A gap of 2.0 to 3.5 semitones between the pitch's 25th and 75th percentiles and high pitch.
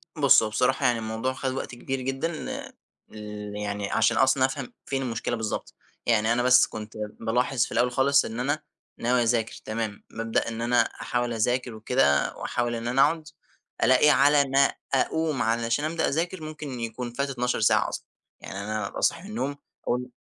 No: average, 3.1 semitones; low, 125 Hz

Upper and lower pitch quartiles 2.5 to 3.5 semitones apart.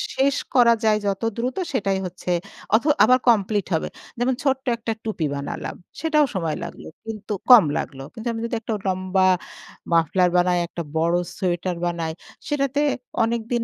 No: average, 5.3 semitones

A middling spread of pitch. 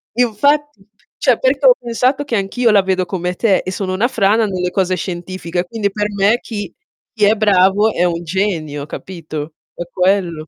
Yes: average, 3.7 semitones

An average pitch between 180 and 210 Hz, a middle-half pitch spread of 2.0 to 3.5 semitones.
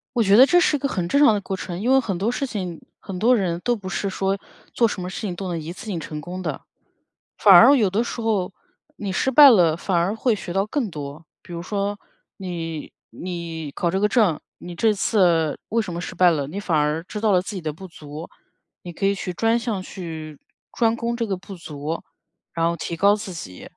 No: high, 190 Hz; average, 4.2 semitones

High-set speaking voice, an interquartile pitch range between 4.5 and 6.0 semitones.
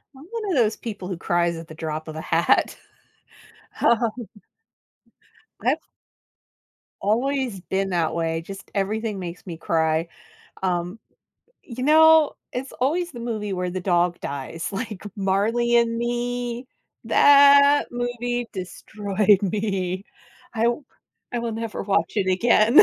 Yes: high, 210 Hz; average, 5.2 semitones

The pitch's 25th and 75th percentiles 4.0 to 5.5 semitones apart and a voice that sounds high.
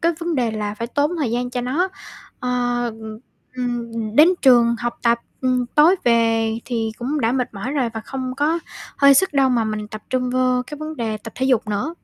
No: average, 3.3 semitones; high, 245 Hz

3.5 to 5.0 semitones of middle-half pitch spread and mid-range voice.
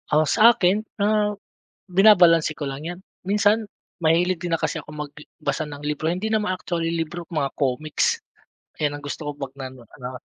Yes: average, 3.9 semitones; medium, 165 Hz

